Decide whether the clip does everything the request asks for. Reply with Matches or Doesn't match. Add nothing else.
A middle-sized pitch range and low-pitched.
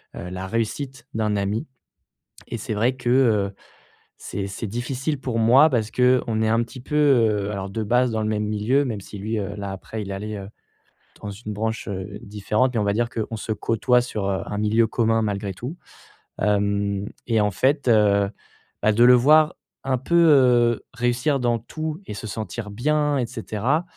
Matches